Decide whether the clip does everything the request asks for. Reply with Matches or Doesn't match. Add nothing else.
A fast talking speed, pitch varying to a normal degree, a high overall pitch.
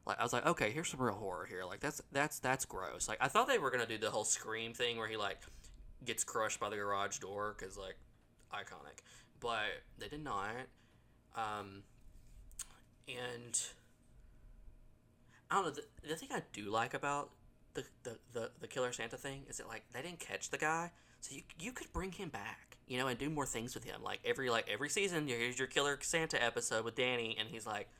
Doesn't match